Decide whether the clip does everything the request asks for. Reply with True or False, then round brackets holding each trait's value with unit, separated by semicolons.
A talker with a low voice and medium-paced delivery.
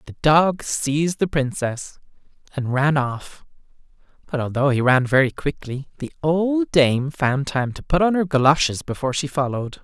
False (145 Hz; 165 wpm)